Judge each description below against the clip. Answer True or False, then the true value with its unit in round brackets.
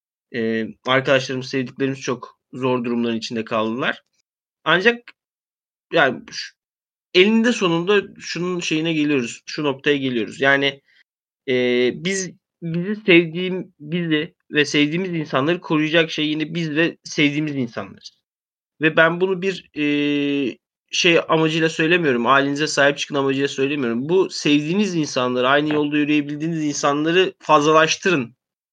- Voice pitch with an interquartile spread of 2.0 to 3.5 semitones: False (3.9 semitones)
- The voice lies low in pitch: False (150 Hz)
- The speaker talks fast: False (115 wpm)